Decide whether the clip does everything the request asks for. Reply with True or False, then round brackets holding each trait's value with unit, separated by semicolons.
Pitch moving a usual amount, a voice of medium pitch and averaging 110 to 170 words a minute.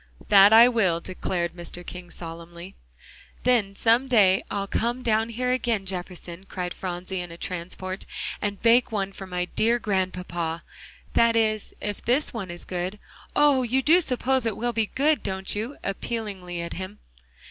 False (4.5 semitones; 195 Hz; 165 wpm)